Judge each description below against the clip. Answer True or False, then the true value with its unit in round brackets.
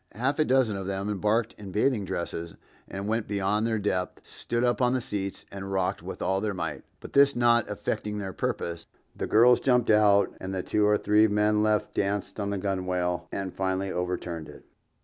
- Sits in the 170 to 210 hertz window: False (105 Hz)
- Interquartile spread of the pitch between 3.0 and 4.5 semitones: False (2.4 semitones)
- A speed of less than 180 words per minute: False (200 wpm)